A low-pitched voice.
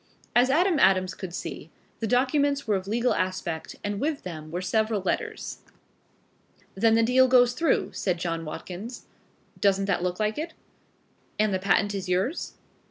No: high, 205 Hz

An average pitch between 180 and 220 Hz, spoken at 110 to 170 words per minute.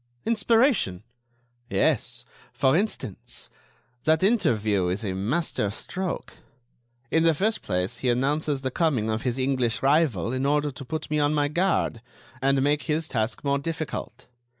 No: medium, 140 Hz; average, 150 wpm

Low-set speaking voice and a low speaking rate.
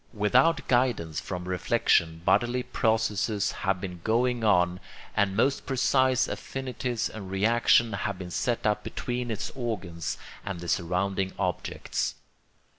Yes: low, 105 Hz; slow, 125 wpm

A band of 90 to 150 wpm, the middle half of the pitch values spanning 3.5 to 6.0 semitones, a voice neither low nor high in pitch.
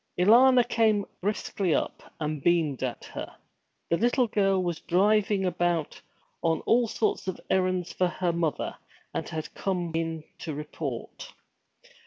Yes: average, 140 wpm; average, 4.1 semitones; medium, 180 Hz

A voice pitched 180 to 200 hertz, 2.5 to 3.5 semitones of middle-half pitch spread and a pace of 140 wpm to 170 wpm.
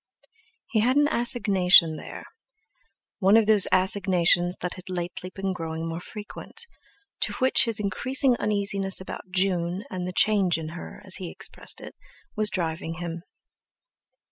Yes: medium, 185 Hz; average, 3.2 semitones; average, 145 wpm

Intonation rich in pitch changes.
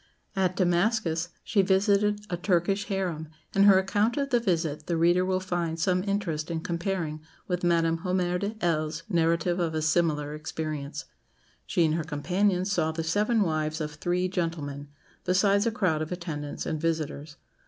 No: average, 3.2 semitones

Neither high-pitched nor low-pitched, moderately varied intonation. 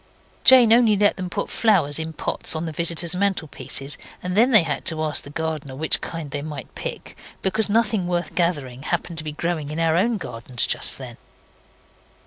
Yes: medium, 165 Hz; average, 4.3 semitones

